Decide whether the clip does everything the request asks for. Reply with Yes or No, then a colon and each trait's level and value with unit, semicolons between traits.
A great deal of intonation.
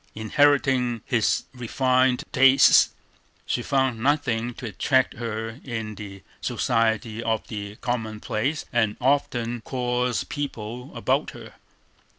No: average, 2.8 semitones